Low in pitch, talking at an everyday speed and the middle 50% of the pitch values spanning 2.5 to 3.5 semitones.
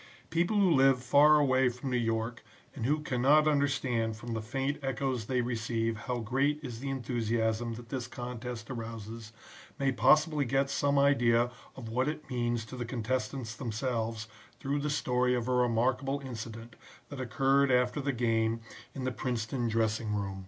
Yes: low, 125 Hz; average, 165 wpm; average, 2.9 semitones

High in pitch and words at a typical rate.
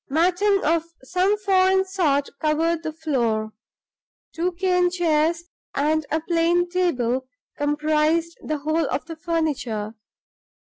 No: very high, 325 Hz; slow, 115 wpm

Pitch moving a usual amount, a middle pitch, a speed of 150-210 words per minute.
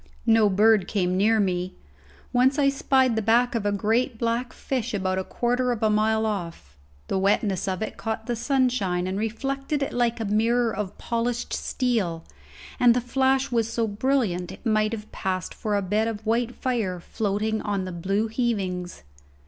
No: average, 3.5 semitones; high, 220 Hz; average, 180 wpm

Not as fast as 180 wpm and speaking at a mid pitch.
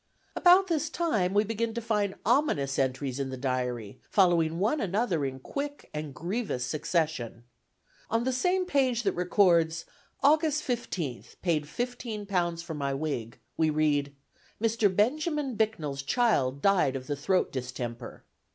Yes: average, 140 wpm; medium, 180 Hz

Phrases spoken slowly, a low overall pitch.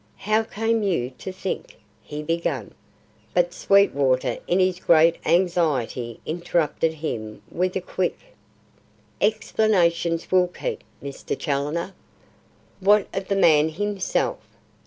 No: slow, 115 wpm; medium, 175 Hz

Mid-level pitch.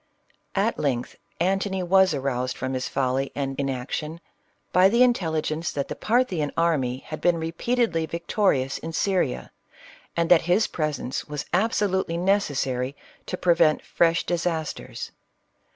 Yes: medium, 165 Hz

